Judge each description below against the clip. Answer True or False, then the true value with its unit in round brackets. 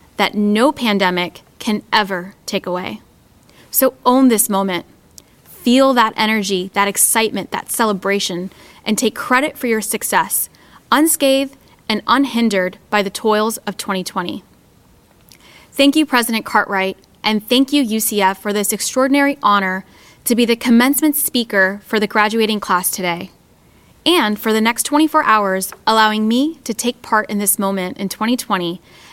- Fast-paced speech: False (145 wpm)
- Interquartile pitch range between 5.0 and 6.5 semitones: False (3.8 semitones)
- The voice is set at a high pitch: True (215 Hz)